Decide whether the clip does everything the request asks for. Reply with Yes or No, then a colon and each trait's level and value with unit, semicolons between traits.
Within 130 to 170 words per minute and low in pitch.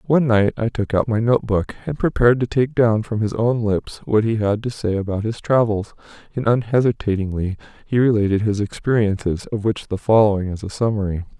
No: average, 200 wpm; low, 110 Hz